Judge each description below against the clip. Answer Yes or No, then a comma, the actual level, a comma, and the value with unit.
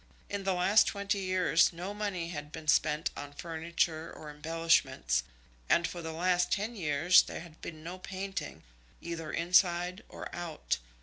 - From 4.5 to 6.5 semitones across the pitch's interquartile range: No, narrow, 2.6 semitones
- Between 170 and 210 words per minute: No, average, 160 wpm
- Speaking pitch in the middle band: Yes, medium, 170 Hz